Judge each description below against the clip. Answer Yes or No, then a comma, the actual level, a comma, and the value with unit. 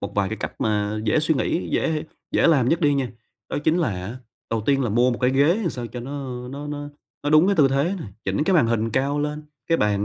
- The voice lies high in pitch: No, low, 135 Hz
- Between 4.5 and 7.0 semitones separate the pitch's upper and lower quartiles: Yes, average, 5.1 semitones